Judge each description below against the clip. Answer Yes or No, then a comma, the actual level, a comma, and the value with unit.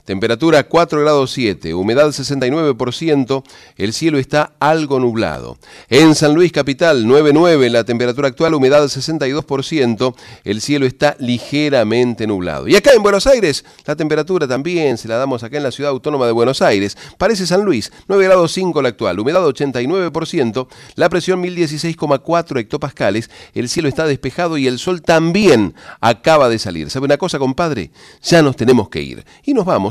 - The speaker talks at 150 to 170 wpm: Yes, average, 165 wpm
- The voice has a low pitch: No, medium, 145 Hz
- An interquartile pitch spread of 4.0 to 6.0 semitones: Yes, average, 4.7 semitones